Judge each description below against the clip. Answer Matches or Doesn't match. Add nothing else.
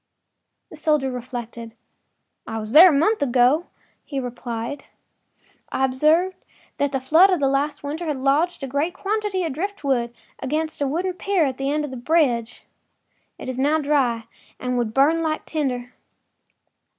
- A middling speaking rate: Matches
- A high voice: Matches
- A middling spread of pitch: Matches